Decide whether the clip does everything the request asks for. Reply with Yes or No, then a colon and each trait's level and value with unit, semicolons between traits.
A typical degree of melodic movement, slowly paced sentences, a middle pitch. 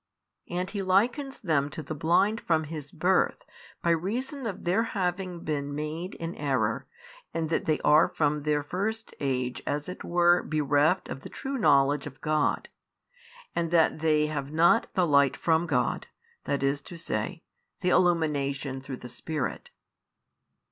No: average, 3.8 semitones; average, 155 wpm; medium, 160 Hz